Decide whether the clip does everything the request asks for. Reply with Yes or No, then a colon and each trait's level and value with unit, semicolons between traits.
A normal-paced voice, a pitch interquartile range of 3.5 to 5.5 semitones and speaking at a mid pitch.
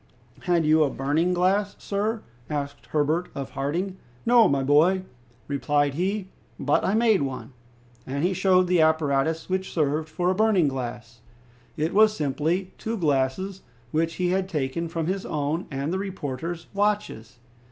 Yes: average, 155 wpm; average, 4.8 semitones; medium, 165 Hz